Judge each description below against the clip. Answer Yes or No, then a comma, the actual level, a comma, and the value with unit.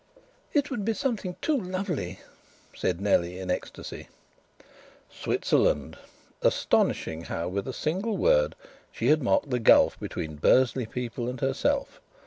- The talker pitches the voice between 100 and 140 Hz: Yes, low, 135 Hz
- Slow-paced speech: Yes, slow, 130 wpm